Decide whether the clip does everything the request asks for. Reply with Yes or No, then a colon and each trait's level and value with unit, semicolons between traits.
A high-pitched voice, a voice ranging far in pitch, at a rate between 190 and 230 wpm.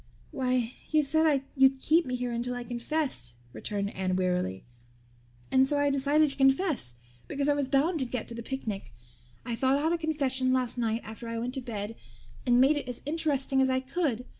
No: very high, 260 Hz; average, 3.6 semitones; average, 200 wpm